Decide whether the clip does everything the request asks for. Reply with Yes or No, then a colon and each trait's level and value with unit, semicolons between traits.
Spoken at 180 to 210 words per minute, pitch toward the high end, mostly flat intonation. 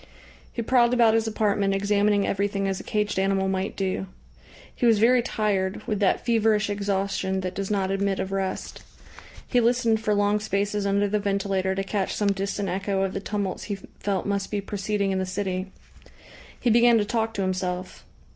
Yes: average, 185 wpm; high, 200 Hz; narrow, 1.7 semitones